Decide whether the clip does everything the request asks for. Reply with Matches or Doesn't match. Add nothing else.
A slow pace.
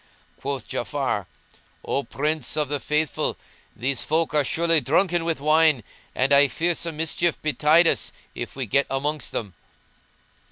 Doesn't match